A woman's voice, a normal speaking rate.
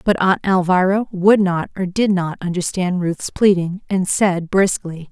Yes: female; average, 165 wpm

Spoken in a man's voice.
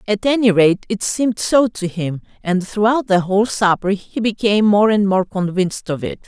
No: female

